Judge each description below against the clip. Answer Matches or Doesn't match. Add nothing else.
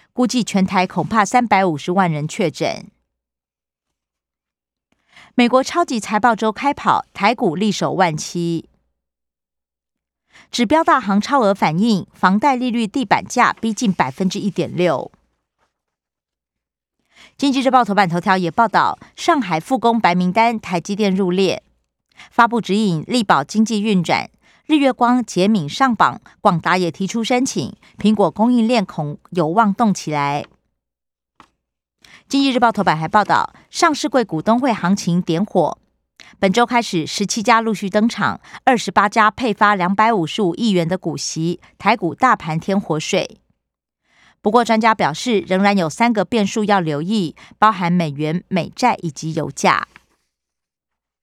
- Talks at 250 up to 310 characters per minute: Doesn't match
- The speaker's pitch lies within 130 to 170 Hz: Doesn't match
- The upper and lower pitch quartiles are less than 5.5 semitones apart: Matches